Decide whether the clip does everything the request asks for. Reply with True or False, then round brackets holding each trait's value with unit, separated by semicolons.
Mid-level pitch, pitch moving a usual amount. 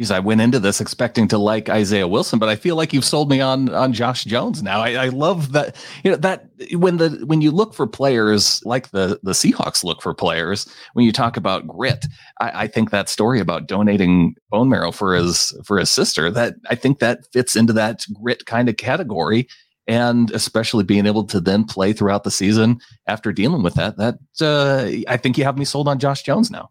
False (120 Hz; 4.4 semitones)